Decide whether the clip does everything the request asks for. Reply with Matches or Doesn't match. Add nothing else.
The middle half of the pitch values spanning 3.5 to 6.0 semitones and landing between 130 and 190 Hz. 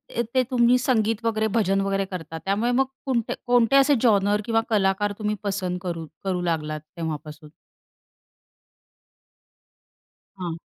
Doesn't match